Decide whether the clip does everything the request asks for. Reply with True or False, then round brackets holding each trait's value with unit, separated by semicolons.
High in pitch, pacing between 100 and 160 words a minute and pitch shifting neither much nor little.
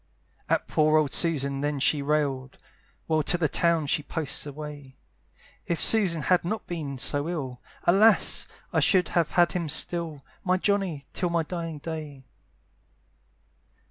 False (155 Hz; 145 wpm; 3.2 semitones)